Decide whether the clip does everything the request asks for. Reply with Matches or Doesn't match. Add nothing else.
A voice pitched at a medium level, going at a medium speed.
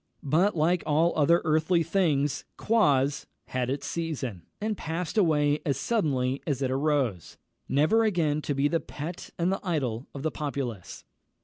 Matches